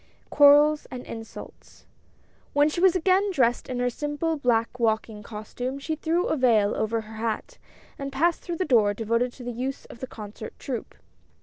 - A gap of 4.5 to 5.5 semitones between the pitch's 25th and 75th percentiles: Yes, average, 4.9 semitones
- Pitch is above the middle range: Yes, very high, 250 Hz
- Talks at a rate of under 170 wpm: No, average, 185 wpm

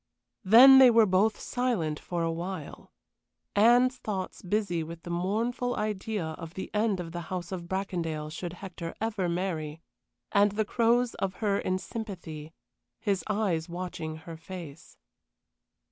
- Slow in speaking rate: No, average, 145 wpm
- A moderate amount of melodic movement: Yes, average, 4.2 semitones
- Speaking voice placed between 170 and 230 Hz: Yes, medium, 185 Hz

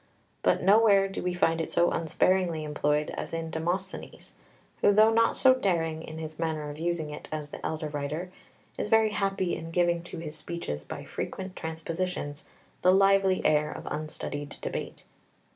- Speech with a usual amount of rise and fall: Yes, average, 3.5 semitones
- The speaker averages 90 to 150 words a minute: No, average, 170 wpm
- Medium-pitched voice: Yes, medium, 165 Hz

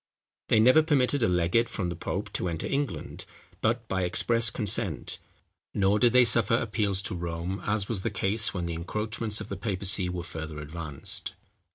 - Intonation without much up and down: No, average, 4.6 semitones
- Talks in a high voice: No, low, 100 Hz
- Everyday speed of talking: Yes, average, 180 wpm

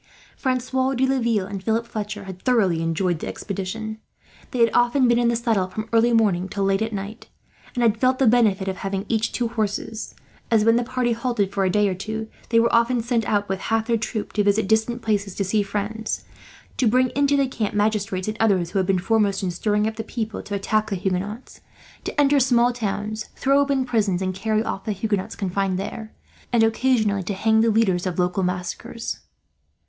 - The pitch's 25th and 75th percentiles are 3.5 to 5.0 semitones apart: No, average, 3.1 semitones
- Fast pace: Yes, fast, 210 wpm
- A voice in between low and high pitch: No, high, 215 Hz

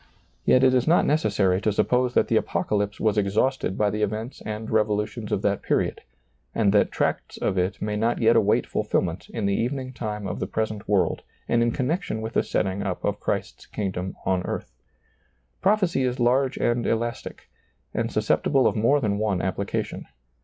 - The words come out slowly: No, average, 180 wpm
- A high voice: No, low, 110 Hz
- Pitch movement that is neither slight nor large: Yes, average, 3.6 semitones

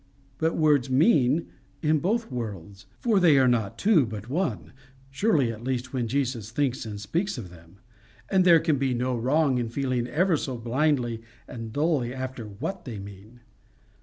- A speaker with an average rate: Yes, average, 170 wpm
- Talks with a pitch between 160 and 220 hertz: No, low, 130 Hz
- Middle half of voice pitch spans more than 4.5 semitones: Yes, average, 5.1 semitones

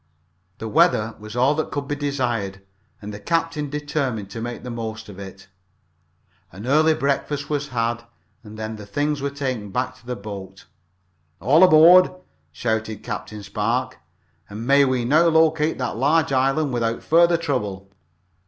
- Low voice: Yes, low, 125 Hz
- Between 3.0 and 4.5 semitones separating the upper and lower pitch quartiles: No, average, 5.3 semitones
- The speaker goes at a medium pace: Yes, average, 160 wpm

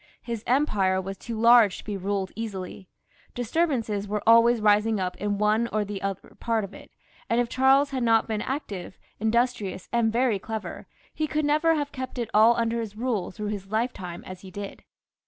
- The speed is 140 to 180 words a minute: No, average, 190 wpm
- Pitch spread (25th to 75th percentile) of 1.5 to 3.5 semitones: Yes, average, 3.1 semitones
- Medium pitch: No, high, 220 Hz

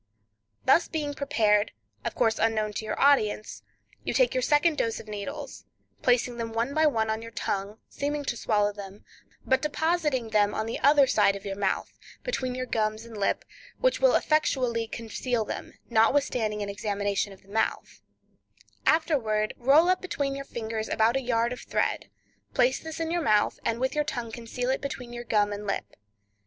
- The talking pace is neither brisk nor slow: Yes, average, 185 wpm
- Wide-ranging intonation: No, average, 4.7 semitones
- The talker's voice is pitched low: No, high, 235 Hz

